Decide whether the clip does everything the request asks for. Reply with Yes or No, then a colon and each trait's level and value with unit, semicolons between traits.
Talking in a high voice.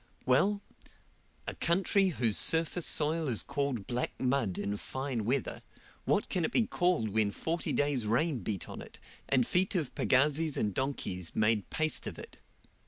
No: low, 135 Hz